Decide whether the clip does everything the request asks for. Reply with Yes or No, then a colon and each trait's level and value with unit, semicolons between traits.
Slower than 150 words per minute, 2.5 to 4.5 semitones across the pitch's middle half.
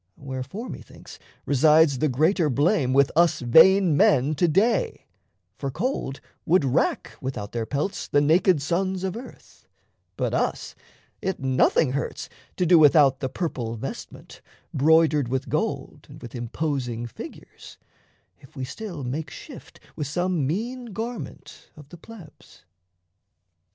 No: slow, 135 wpm; average, 5.3 semitones